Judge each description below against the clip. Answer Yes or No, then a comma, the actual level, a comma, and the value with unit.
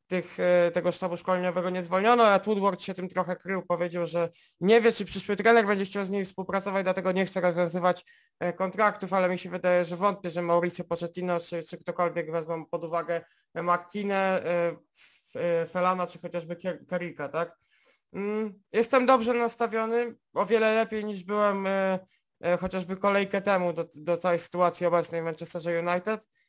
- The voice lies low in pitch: No, medium, 180 Hz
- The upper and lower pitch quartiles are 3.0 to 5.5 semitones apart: No, narrow, 2.4 semitones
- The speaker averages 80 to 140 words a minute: No, average, 155 wpm